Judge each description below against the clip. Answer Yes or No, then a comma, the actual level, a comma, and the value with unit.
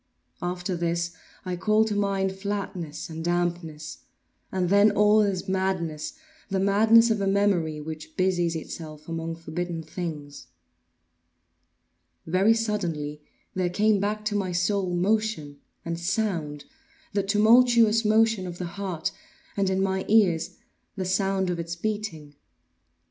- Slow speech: Yes, slow, 125 wpm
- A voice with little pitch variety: No, average, 3.7 semitones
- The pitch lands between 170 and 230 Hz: Yes, high, 190 Hz